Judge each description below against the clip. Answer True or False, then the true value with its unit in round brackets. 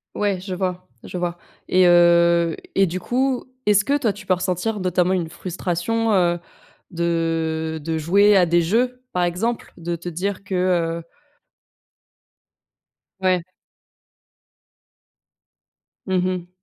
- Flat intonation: True (2.3 semitones)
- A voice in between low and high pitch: True (180 Hz)